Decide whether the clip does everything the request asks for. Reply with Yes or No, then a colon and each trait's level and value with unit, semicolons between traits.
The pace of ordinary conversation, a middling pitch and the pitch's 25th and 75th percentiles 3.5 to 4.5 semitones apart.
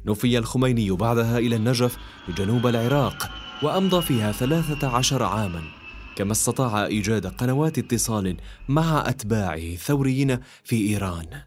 No: average, 115 wpm; low, 115 Hz; average, 3.9 semitones